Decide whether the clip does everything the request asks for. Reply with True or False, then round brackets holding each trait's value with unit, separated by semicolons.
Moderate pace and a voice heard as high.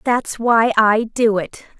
True (165 wpm; 220 Hz)